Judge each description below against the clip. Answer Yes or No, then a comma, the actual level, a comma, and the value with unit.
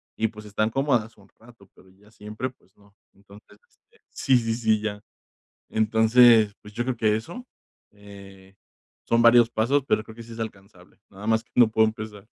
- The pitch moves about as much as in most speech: No, narrow, 2.2 semitones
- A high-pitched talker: No, low, 110 Hz